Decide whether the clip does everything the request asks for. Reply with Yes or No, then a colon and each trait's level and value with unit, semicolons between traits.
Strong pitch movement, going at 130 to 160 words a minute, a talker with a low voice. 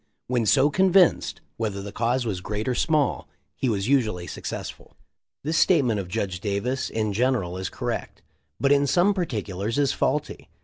No: wide, 5.7 semitones; average, 170 wpm; low, 120 Hz